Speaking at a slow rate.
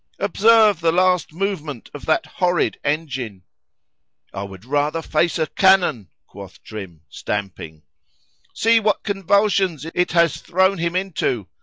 Yes: slow, 120 wpm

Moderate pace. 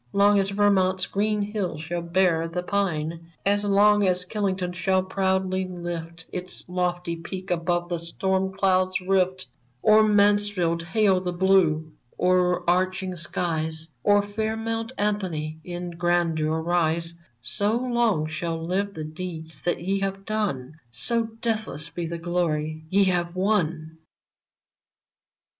No: slow, 130 wpm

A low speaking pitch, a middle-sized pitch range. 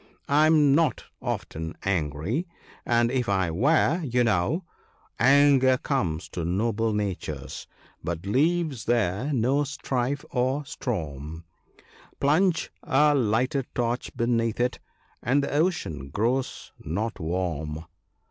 No: low, 120 Hz; wide, 7.5 semitones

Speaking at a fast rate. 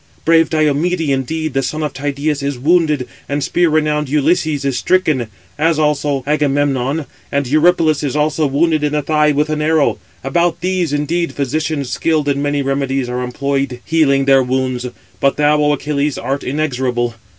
No: average, 165 wpm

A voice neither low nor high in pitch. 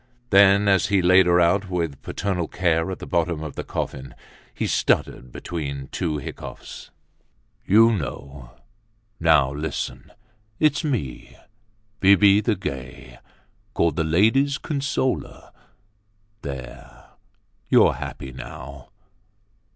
No: very low, 90 Hz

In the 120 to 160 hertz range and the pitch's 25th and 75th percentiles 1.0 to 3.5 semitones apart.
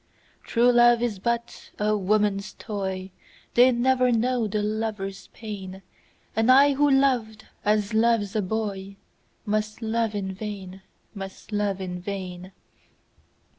No: high, 215 Hz; average, 3.2 semitones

